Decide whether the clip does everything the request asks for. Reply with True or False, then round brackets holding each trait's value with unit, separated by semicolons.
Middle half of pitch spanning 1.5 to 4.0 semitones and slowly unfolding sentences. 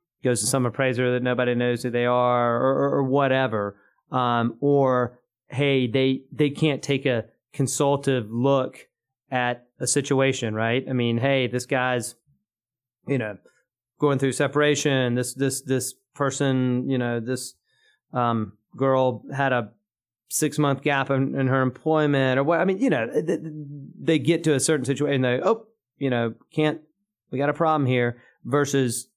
False (2.5 semitones; 165 wpm)